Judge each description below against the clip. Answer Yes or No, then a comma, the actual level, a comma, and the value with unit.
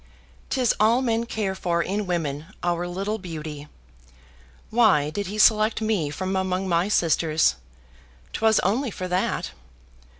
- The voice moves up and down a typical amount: Yes, average, 4.2 semitones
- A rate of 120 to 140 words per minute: Yes, slow, 135 wpm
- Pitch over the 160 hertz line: Yes, high, 190 Hz